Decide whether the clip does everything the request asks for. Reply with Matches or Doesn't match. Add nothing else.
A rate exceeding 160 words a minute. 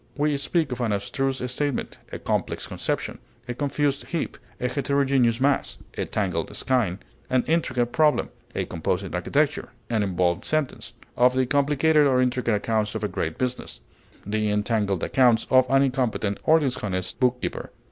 Doesn't match